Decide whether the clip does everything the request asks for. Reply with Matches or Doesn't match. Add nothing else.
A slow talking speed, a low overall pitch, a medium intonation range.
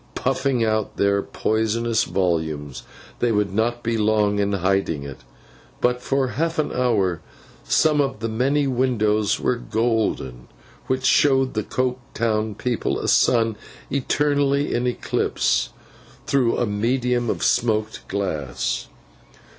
Matches